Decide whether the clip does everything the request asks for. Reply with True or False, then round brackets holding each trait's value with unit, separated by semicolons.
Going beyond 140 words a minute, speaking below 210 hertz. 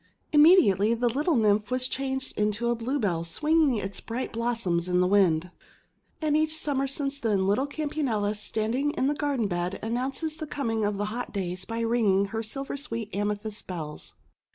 False (180 wpm; 230 Hz)